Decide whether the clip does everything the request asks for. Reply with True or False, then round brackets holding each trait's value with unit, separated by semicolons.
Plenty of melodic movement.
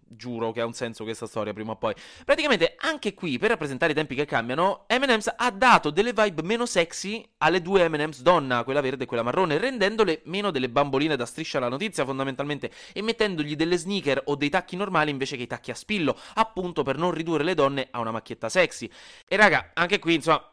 True (7.4 semitones)